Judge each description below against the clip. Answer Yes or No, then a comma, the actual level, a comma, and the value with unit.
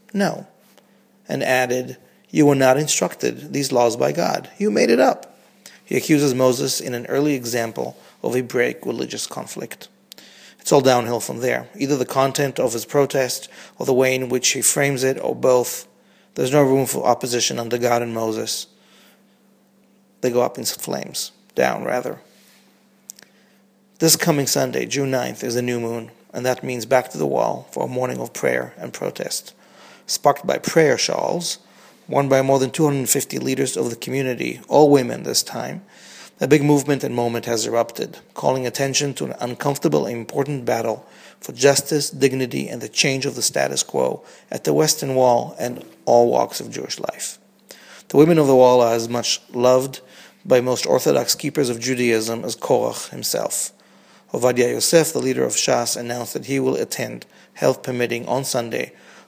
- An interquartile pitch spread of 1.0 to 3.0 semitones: Yes, narrow, 2.6 semitones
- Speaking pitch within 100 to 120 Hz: No, low, 130 Hz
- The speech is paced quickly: No, average, 175 wpm